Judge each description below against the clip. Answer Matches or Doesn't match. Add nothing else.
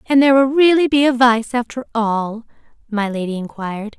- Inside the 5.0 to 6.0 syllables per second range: Matches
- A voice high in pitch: Matches